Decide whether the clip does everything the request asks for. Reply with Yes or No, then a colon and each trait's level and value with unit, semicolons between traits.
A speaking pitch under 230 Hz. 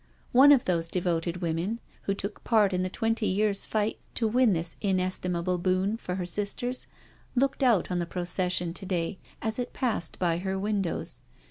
Yes: high, 190 Hz